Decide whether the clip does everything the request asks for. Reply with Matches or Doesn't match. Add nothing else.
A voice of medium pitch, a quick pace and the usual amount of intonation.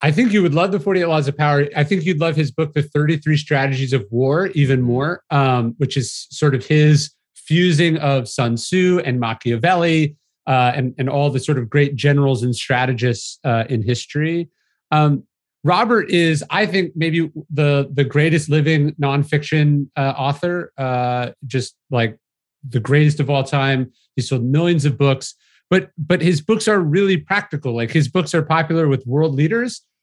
Doesn't match